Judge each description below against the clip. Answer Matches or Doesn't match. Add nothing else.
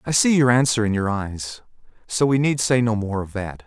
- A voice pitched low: Matches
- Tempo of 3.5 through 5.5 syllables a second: Matches